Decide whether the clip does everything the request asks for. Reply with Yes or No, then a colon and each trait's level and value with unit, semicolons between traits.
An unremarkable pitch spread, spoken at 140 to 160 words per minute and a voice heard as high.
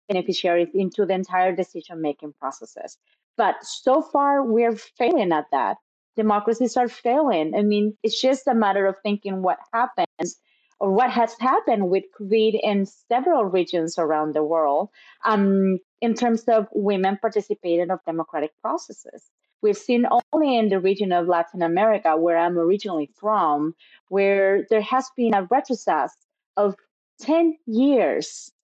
Yes: average, 4.4 semitones; average, 145 wpm; high, 205 Hz